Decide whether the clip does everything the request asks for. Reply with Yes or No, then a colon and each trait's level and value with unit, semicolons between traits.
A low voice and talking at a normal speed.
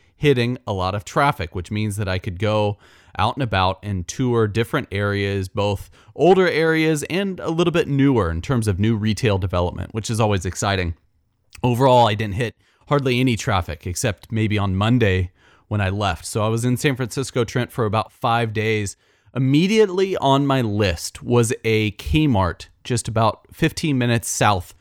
Yes: low, 110 Hz; average, 175 wpm